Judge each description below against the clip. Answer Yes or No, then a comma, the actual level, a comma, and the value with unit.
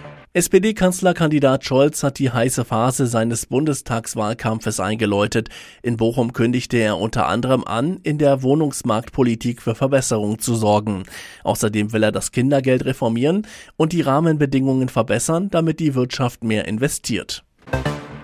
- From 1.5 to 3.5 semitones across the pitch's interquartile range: No, average, 3.9 semitones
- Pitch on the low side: Yes, low, 125 Hz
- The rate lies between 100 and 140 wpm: Yes, slow, 125 wpm